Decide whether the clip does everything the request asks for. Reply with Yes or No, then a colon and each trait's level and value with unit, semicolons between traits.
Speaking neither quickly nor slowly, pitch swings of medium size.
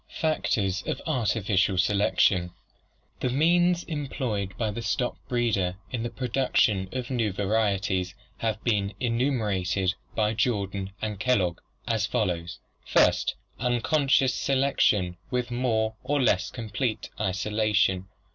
No: slow, 120 wpm; average, 4.4 semitones